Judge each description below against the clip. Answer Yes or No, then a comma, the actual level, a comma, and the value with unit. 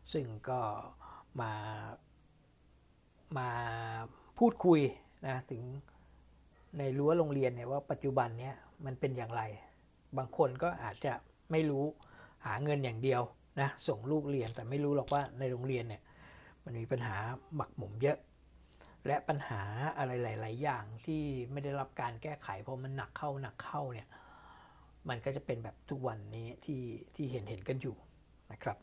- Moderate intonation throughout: Yes, average, 3.8 semitones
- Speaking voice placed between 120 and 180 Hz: Yes, low, 130 Hz